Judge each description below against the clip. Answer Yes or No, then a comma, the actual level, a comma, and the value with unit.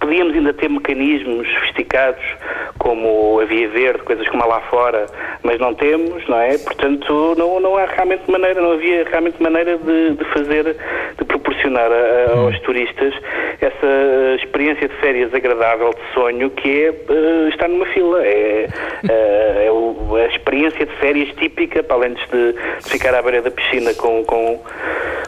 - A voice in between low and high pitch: Yes, medium, 150 Hz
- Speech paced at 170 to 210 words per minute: No, average, 160 wpm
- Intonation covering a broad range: Yes, wide, 7.2 semitones